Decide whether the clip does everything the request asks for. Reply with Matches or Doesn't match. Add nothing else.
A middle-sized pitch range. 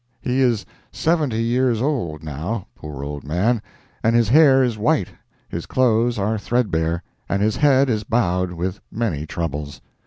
Doesn't match